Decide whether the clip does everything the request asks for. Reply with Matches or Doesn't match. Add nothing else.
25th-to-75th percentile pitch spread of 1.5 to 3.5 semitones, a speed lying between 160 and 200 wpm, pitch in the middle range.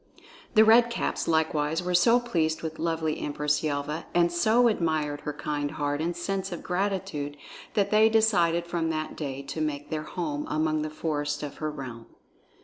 Matches